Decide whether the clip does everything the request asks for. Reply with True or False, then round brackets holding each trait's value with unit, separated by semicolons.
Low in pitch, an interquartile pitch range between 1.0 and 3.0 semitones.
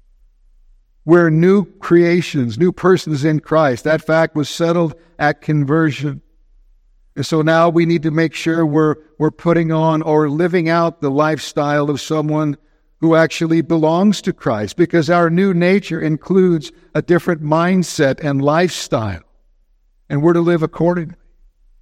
False (160 Hz; 2.5 semitones)